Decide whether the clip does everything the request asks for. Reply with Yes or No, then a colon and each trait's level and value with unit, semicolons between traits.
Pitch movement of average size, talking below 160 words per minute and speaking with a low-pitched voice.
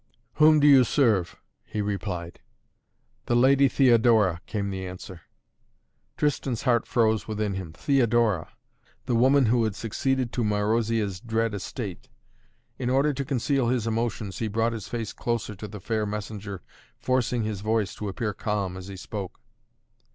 Yes: average, 3.2 semitones; average, 150 wpm; low, 110 Hz